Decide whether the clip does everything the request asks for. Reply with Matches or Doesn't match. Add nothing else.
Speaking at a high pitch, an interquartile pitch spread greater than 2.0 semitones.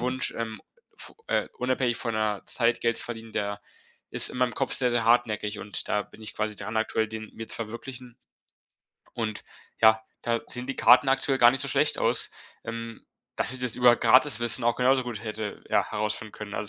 Doesn't match